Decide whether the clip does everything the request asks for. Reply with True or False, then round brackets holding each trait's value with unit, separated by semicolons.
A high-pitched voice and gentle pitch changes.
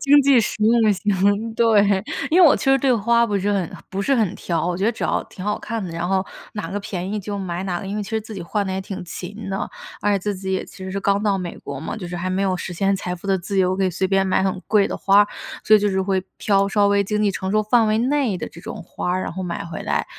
True (195 Hz; 2.3 semitones)